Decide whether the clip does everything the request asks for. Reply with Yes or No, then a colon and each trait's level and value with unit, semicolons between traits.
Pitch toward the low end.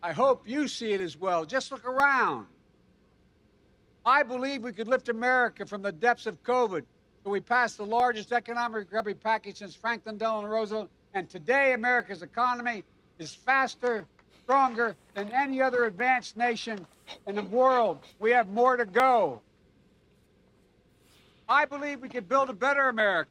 No: high, 240 Hz